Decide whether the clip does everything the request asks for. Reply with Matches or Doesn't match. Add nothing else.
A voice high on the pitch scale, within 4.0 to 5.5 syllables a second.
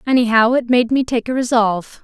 Doesn't match